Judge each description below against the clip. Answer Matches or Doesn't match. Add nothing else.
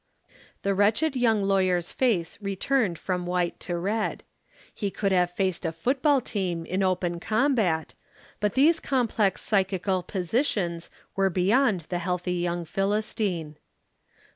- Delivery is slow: Matches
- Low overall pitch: Doesn't match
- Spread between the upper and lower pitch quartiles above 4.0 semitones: Doesn't match